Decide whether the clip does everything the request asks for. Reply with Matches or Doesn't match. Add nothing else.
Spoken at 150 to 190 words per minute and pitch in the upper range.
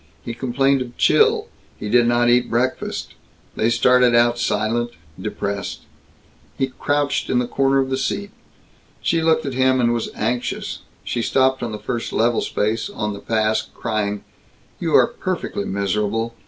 Doesn't match